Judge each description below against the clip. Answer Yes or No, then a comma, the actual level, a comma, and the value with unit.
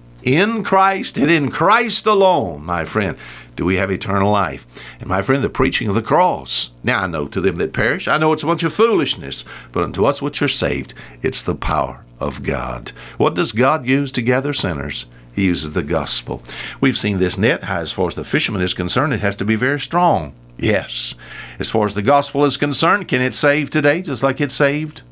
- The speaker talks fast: Yes, fast, 215 wpm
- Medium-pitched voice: No, low, 120 Hz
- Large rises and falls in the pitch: Yes, wide, 8.3 semitones